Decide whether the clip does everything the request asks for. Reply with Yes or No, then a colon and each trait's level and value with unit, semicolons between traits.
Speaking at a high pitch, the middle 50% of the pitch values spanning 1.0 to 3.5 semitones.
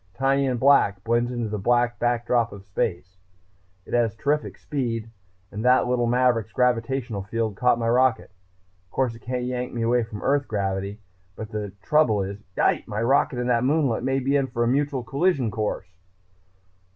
No: low, 120 Hz; average, 2.8 semitones